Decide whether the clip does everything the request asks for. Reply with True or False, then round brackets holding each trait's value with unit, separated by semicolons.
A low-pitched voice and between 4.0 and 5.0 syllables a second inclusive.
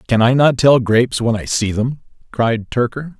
True (120 Hz; 4.8 syllables/s)